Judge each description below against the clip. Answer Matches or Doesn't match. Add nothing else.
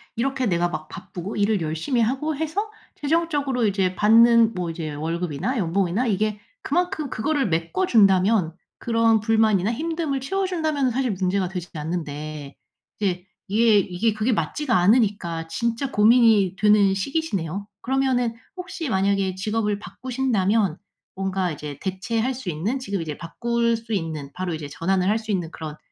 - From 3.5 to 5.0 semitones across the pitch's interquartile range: Doesn't match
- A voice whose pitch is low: Doesn't match